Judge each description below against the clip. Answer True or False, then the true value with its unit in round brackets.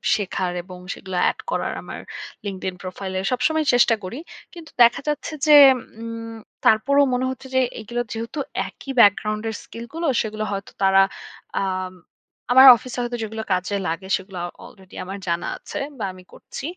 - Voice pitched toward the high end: True (220 Hz)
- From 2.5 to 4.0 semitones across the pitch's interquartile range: False (4.5 semitones)